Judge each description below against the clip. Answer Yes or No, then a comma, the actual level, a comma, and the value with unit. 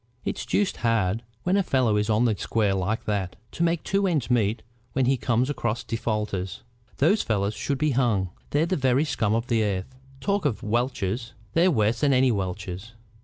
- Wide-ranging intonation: No, average, 4.7 semitones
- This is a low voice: Yes, low, 115 Hz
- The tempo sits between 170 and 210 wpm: Yes, average, 190 wpm